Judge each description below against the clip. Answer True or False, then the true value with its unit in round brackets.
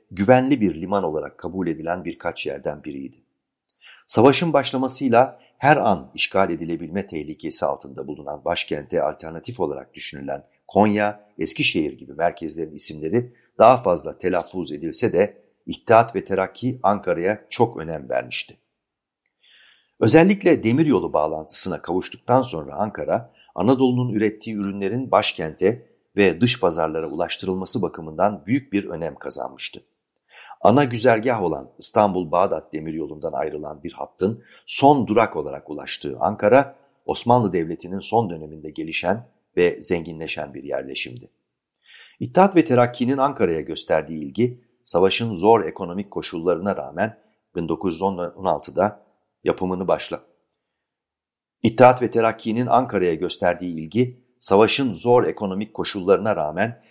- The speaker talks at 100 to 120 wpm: True (110 wpm)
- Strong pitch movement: True (6.5 semitones)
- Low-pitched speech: True (100 Hz)